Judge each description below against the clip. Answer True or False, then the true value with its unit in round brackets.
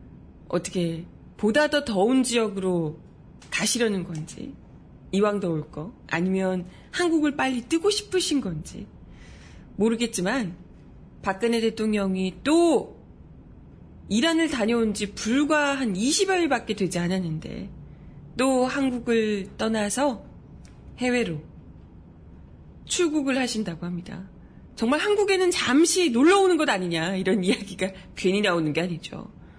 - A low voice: False (215 Hz)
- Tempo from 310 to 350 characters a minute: False (245 characters per minute)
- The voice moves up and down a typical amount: False (7.1 semitones)